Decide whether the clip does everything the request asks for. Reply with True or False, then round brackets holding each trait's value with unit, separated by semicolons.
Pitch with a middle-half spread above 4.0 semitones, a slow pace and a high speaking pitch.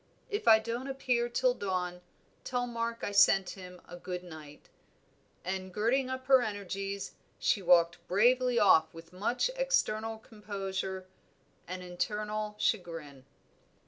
True (4.6 semitones; 130 wpm; 205 Hz)